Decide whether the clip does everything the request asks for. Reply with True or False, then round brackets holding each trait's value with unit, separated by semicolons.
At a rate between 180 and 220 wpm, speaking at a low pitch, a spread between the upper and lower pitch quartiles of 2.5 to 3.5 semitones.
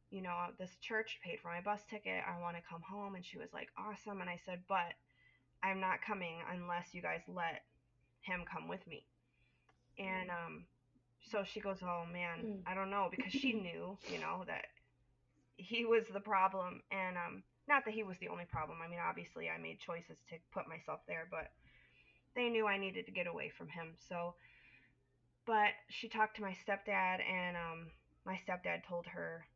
False (195 wpm; 185 Hz; 3.2 semitones)